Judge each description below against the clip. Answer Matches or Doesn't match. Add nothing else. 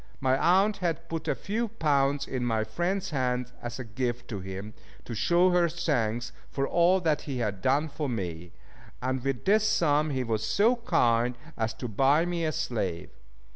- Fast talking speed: Doesn't match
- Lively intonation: Matches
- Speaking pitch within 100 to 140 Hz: Matches